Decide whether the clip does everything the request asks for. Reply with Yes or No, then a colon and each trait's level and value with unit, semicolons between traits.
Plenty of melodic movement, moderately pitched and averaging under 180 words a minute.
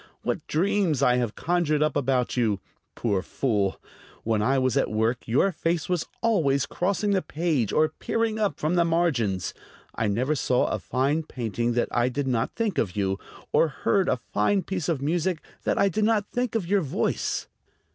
No: wide, 6.9 semitones; medium, 145 Hz; average, 185 wpm